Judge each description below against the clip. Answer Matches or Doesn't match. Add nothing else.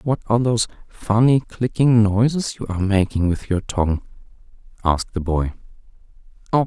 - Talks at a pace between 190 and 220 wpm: Doesn't match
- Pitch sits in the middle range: Doesn't match